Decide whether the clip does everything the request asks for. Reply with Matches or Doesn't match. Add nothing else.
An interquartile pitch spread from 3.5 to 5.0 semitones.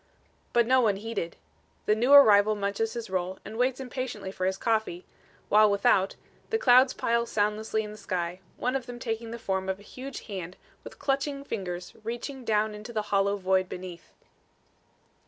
Matches